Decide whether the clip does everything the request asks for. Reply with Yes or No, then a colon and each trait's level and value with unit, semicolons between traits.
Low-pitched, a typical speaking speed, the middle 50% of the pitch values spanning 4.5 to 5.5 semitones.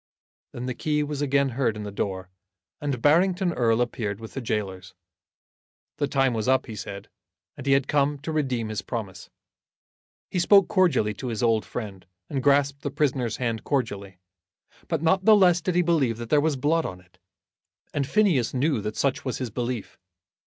Yes: low, 130 Hz; average, 190 wpm; average, 5.0 semitones